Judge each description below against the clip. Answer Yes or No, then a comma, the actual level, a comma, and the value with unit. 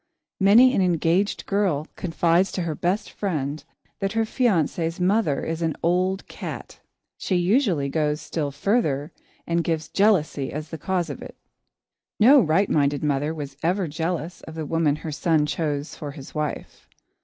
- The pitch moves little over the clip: No, average, 4.1 semitones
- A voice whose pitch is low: No, medium, 165 Hz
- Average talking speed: Yes, average, 160 wpm